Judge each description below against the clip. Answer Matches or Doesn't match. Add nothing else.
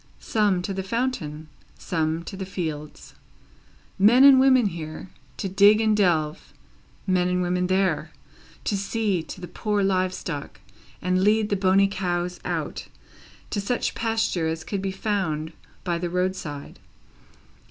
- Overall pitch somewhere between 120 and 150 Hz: Doesn't match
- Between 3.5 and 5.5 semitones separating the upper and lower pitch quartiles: Doesn't match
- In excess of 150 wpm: Doesn't match